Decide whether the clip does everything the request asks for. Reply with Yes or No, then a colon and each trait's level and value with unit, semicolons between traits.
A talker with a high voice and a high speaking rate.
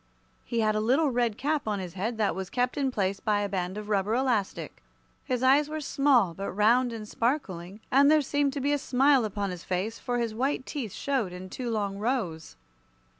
Yes: high, 230 Hz; fast, 215 wpm